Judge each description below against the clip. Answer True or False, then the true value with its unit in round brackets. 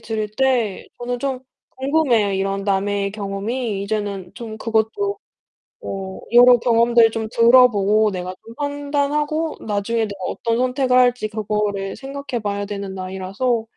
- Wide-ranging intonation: False (3.9 semitones)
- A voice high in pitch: True (220 Hz)